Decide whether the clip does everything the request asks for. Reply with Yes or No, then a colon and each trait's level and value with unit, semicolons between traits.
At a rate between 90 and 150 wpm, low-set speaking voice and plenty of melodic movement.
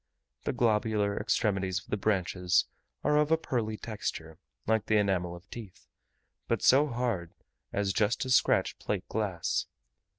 No: average, 145 wpm; low, 105 Hz; average, 3.5 semitones